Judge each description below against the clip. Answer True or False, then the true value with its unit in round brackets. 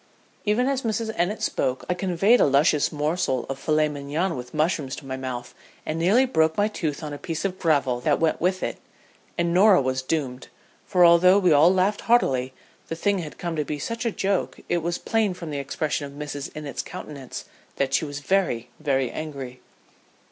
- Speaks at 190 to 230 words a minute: True (200 wpm)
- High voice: False (160 Hz)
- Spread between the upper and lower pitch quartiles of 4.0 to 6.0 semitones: True (4.9 semitones)